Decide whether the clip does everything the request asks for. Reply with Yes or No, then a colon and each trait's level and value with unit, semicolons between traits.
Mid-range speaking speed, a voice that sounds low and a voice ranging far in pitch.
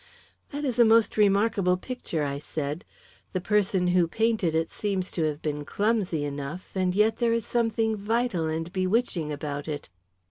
No: average, 170 wpm; medium, 185 Hz; wide, 5.8 semitones